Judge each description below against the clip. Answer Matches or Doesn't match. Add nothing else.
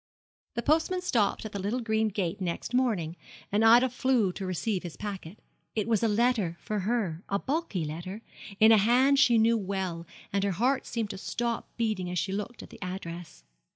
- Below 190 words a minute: Doesn't match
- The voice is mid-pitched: Doesn't match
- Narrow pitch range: Doesn't match